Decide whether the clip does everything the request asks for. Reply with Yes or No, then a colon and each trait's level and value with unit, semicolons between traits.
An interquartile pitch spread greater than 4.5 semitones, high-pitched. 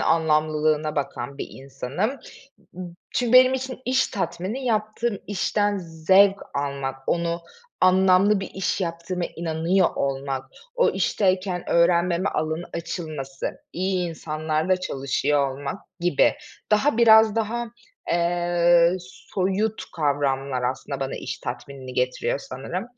No: average, 4.9 semitones; medium, 170 Hz